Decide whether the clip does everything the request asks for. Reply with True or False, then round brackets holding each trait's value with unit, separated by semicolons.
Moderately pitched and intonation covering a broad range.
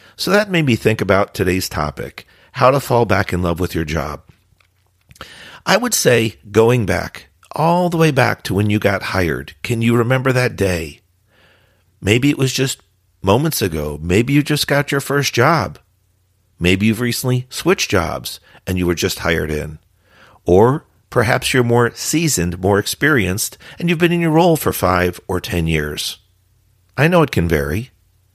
False (100 Hz; 5.9 semitones)